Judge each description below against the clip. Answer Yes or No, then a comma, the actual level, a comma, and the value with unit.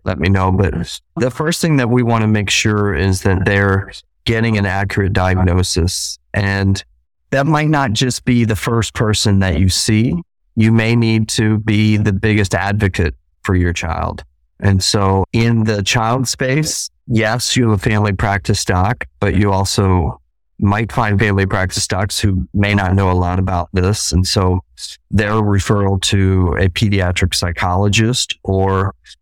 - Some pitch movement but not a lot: Yes, average, 3.0 semitones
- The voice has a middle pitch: No, low, 100 Hz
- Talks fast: No, average, 165 wpm